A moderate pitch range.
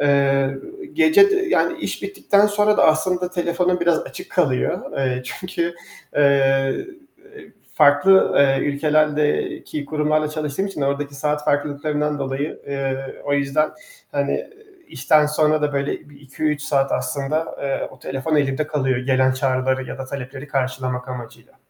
No: narrow, 2.3 semitones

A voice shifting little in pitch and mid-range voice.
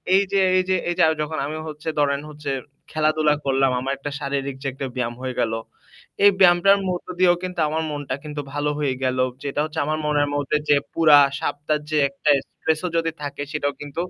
Yes: narrow, 2.0 semitones; medium, 150 Hz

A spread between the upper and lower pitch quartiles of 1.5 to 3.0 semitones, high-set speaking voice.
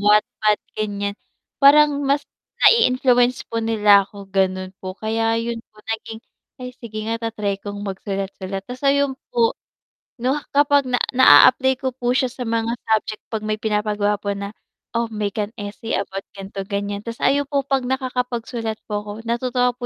No: average, 3.7 semitones; high, 225 Hz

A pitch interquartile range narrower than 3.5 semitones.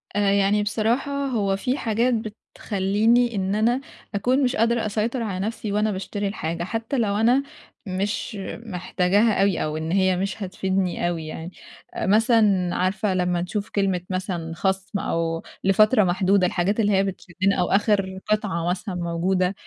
Yes: average, 2.9 semitones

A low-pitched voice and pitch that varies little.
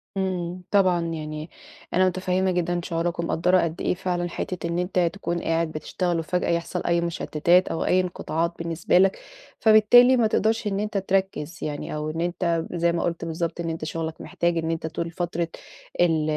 No: medium, 170 Hz; narrow, 1.9 semitones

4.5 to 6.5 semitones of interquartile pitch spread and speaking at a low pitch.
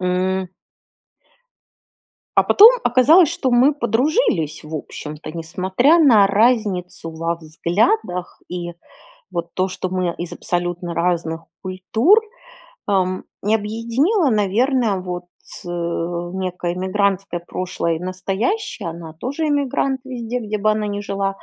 No: wide, 5.4 semitones; high, 190 Hz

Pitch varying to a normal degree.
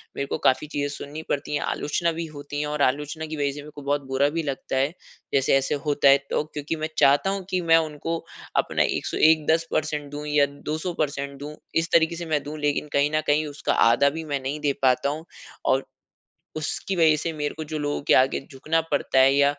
No: narrow, 1.7 semitones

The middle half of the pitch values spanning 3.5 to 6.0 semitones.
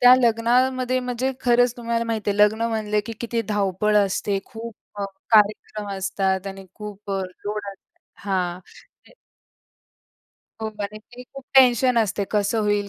No: average, 2.9 semitones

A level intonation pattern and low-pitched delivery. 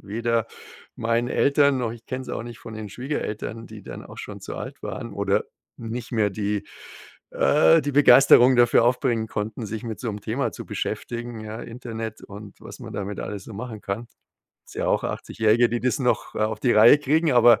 Yes: narrow, 2.3 semitones; low, 115 Hz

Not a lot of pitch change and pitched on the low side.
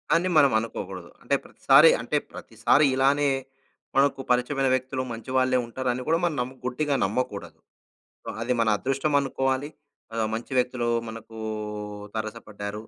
No: average, 3.1 semitones; low, 130 Hz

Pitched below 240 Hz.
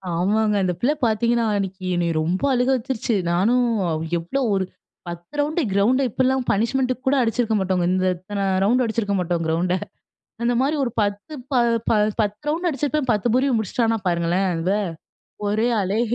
Yes: high, 220 Hz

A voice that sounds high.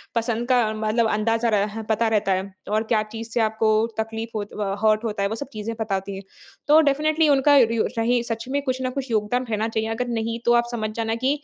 Yes: high, 225 Hz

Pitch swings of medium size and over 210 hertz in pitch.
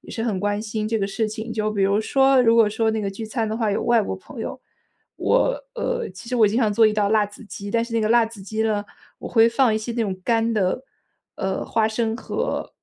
No: narrow, 1.8 semitones; high, 220 Hz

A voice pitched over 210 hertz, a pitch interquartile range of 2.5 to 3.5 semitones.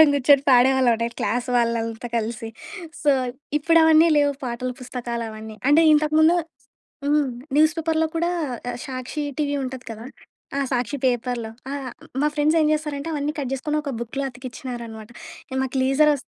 No: very high, 265 Hz; average, 3.9 semitones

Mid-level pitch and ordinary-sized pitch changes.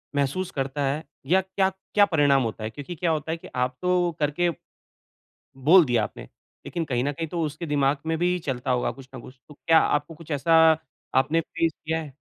Yes: medium, 150 Hz; average, 3.7 semitones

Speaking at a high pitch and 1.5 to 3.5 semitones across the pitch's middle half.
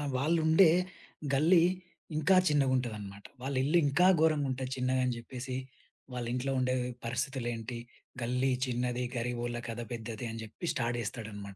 No: low, 125 Hz; narrow, 2.6 semitones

